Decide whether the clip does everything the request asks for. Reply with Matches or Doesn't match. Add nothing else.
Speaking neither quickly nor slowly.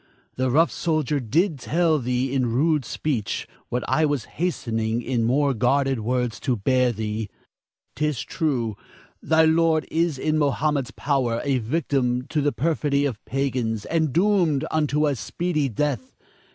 Matches